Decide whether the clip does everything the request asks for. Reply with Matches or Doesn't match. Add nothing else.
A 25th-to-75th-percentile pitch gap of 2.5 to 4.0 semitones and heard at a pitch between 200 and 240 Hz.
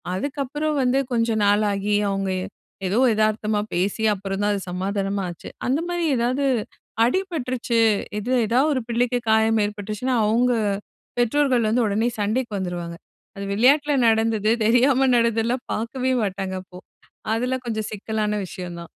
Matches